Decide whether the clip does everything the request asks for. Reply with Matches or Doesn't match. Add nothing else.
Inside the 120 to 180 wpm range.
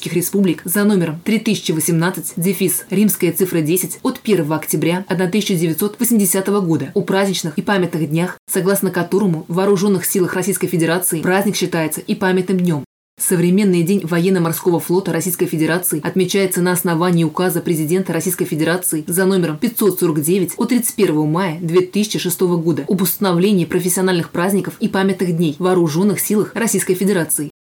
Matches